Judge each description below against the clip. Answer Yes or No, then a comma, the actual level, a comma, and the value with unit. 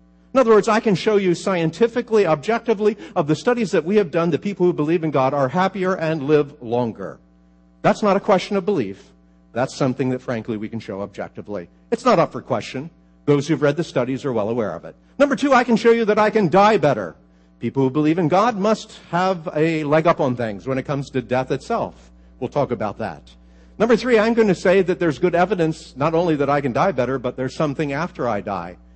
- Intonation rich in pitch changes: Yes, wide, 8.5 semitones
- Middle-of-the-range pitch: Yes, medium, 155 Hz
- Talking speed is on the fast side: Yes, fast, 230 wpm